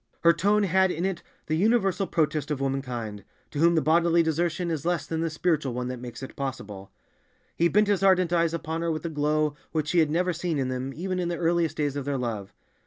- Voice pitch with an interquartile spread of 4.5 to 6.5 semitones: No, average, 3.8 semitones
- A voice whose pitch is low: No, medium, 160 Hz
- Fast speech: Yes, fast, 235 wpm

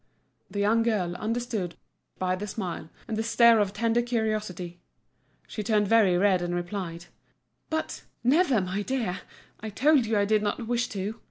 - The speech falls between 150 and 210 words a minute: Yes, average, 160 wpm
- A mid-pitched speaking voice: No, high, 210 Hz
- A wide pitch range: No, average, 3.7 semitones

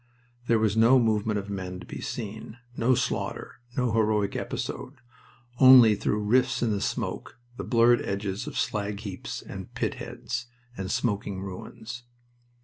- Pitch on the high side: No, low, 110 Hz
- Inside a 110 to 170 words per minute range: Yes, average, 150 wpm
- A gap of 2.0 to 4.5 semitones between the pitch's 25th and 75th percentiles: Yes, average, 2.8 semitones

